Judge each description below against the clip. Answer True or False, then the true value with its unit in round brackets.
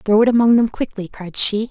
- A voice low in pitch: False (215 Hz)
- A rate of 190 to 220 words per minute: False (245 wpm)